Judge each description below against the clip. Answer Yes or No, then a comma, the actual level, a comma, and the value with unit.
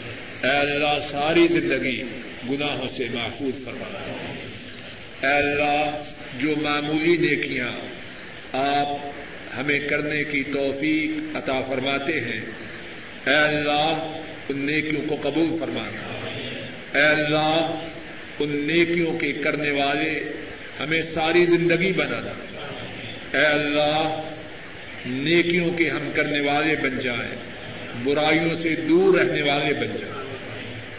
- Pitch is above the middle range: No, medium, 150 Hz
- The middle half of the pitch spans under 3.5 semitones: Yes, narrow, 2.5 semitones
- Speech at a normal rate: No, slow, 105 wpm